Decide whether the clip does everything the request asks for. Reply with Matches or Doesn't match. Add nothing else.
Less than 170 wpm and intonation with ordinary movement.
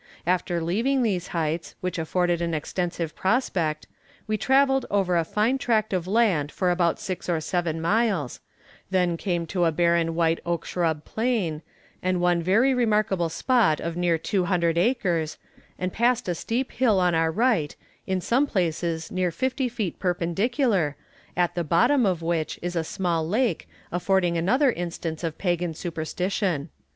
Matches